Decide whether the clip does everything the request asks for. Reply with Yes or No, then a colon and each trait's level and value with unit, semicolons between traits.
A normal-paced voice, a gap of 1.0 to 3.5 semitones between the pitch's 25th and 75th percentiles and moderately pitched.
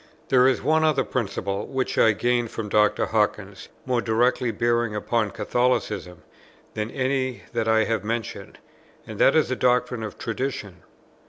No: average, 155 wpm; average, 2.9 semitones; low, 120 Hz